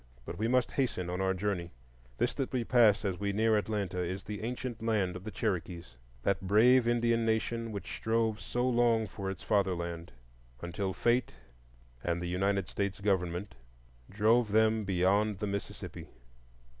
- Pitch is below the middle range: Yes, low, 100 Hz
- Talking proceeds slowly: No, average, 155 wpm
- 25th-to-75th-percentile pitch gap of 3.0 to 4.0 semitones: Yes, average, 3.4 semitones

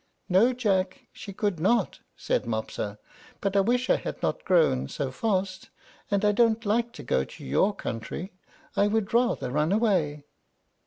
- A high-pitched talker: Yes, high, 195 Hz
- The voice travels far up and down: Yes, wide, 6.5 semitones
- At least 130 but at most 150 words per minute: No, average, 165 wpm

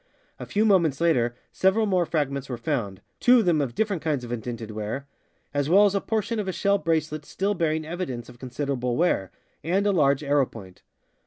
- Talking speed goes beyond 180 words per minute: Yes, average, 200 wpm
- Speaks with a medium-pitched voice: Yes, medium, 150 Hz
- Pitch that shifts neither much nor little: No, wide, 7.1 semitones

